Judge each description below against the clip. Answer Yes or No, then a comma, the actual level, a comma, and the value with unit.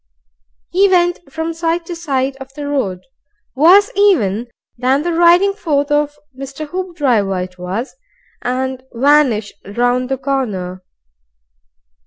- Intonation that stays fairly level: No, wide, 5.4 semitones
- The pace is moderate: No, slow, 125 wpm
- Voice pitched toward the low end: No, very high, 275 Hz